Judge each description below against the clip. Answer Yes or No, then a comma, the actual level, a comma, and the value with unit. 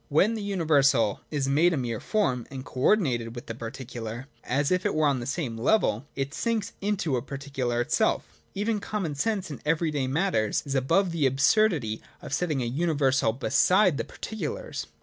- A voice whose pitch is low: No, medium, 145 Hz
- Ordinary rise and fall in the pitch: No, wide, 6.3 semitones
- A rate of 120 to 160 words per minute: No, average, 185 wpm